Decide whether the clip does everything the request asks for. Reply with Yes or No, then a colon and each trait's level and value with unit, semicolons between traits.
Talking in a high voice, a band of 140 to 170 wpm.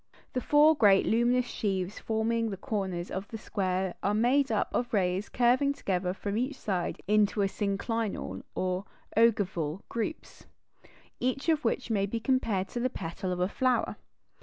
Yes: high, 215 Hz; average, 160 wpm